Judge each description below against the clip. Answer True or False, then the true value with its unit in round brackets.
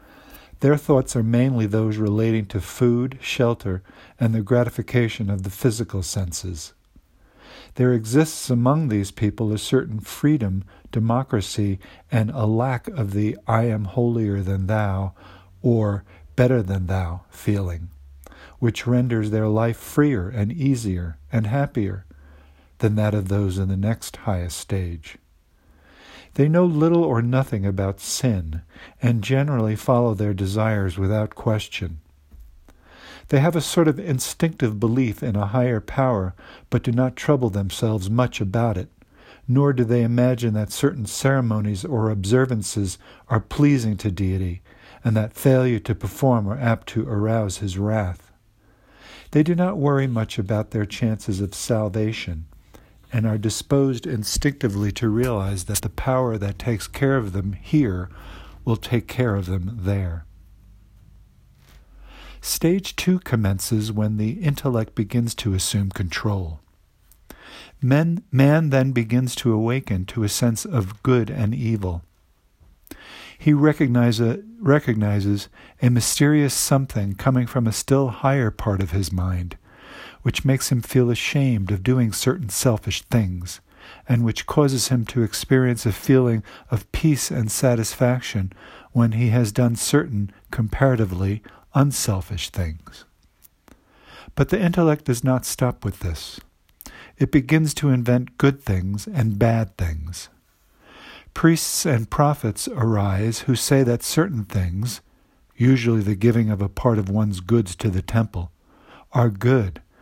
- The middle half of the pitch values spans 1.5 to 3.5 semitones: False (4.3 semitones)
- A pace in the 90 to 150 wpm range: True (140 wpm)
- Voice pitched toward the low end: True (110 Hz)